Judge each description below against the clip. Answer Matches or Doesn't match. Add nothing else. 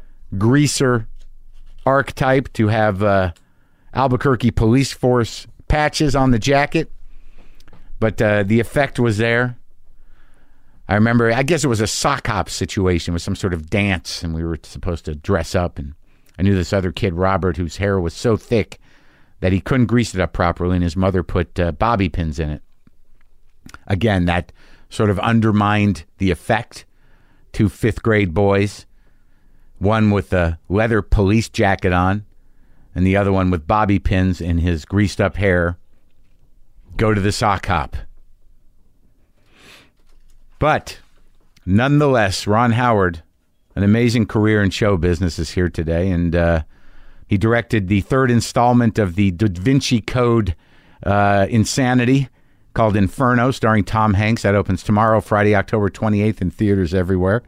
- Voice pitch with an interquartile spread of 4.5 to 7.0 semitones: Doesn't match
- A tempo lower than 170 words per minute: Matches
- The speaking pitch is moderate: Doesn't match